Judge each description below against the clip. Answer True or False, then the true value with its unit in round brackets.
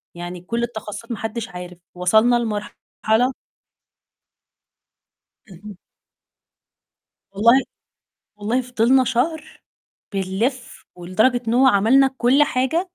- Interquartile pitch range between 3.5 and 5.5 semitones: True (3.9 semitones)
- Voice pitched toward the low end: False (230 Hz)